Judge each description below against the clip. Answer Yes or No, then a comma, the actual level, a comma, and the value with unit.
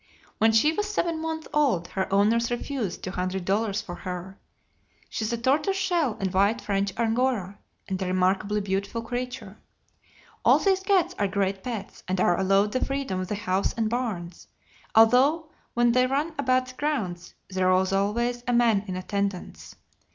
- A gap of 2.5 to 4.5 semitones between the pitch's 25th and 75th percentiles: No, average, 5.0 semitones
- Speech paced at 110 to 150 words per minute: No, average, 175 wpm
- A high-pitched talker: Yes, high, 220 Hz